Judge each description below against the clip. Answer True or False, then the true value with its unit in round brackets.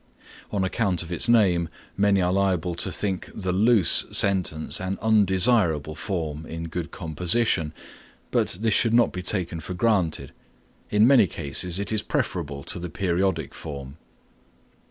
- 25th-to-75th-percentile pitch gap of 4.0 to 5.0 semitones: False (3.6 semitones)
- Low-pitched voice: True (90 Hz)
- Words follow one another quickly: False (150 wpm)